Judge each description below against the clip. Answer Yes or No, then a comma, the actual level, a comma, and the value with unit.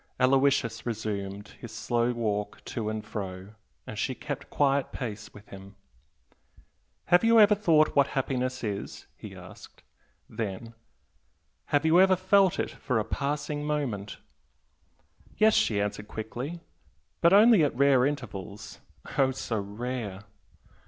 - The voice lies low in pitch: Yes, low, 125 Hz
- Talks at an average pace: No, slow, 130 wpm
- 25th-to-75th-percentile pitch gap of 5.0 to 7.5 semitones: Yes, wide, 5.6 semitones